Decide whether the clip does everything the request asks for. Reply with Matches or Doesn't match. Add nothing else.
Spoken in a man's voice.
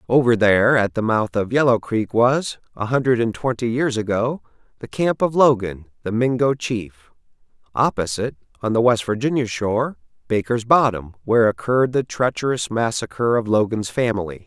Matches